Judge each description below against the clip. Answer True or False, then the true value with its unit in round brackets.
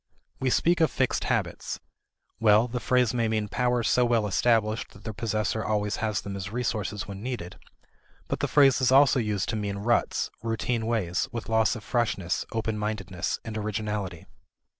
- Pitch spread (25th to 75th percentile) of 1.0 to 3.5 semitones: True (2.6 semitones)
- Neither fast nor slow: True (175 wpm)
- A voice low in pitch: True (110 Hz)